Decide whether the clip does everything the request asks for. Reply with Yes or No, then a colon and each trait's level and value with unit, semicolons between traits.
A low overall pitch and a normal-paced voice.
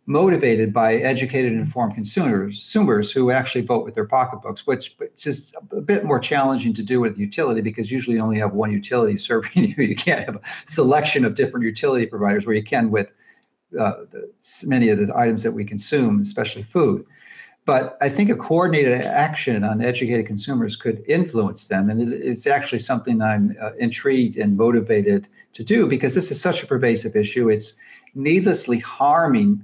Yes: low, 125 Hz; average, 185 wpm